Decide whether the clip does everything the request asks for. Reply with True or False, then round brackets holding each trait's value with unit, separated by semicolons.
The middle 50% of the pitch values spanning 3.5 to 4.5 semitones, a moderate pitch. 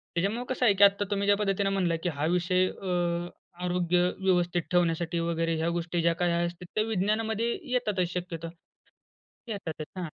False (2.8 semitones; 180 Hz)